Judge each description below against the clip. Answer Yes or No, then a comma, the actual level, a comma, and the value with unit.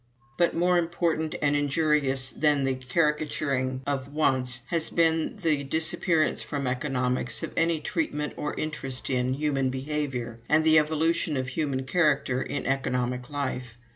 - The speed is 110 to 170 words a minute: Yes, average, 140 wpm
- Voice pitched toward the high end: No, medium, 145 Hz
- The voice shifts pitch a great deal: No, average, 3.3 semitones